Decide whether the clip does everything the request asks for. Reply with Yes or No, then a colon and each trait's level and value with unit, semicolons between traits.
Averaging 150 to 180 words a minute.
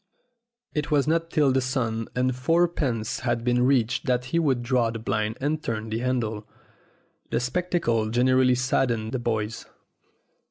Yes: average, 160 wpm